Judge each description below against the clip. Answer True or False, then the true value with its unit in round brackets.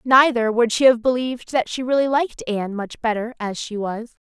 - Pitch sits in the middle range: False (240 Hz)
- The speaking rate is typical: False (210 wpm)